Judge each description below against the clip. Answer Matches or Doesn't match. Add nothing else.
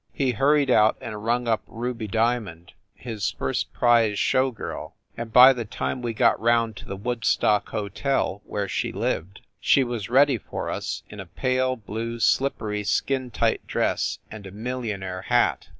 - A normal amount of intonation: Matches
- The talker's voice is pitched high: Doesn't match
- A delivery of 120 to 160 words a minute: Doesn't match